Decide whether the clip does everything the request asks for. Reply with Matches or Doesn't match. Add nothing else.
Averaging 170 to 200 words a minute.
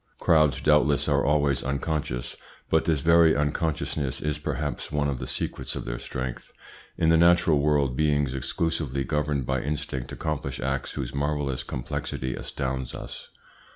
Doesn't match